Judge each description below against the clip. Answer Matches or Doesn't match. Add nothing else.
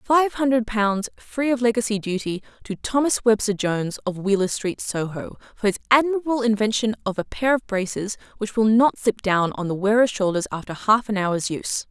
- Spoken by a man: Doesn't match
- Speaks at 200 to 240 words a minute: Doesn't match